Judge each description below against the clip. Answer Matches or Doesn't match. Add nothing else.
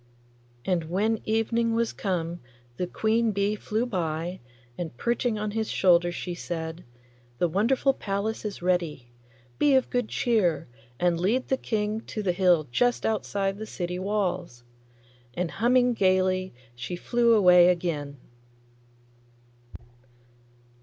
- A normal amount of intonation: Matches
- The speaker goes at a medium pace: Doesn't match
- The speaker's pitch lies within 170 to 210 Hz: Matches